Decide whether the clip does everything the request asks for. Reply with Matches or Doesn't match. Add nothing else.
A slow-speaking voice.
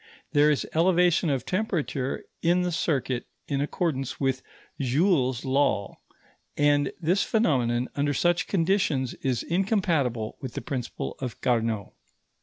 Matches